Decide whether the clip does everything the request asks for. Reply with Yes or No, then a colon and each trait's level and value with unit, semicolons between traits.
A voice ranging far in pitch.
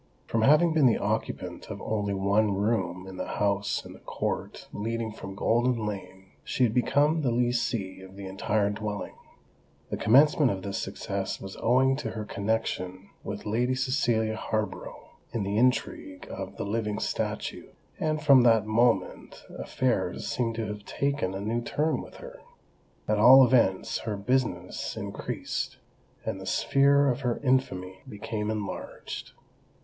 No: average, 4.2 semitones